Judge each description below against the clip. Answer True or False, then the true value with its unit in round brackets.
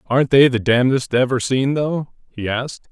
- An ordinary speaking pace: True (185 wpm)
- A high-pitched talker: False (130 Hz)